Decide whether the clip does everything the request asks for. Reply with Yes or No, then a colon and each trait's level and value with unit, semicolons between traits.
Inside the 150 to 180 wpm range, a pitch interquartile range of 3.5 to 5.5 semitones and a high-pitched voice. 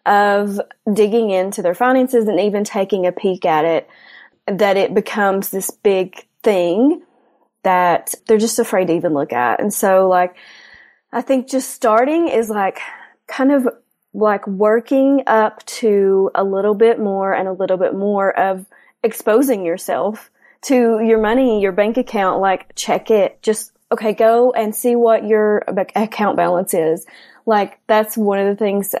No: average, 165 wpm; average, 3.1 semitones; high, 210 Hz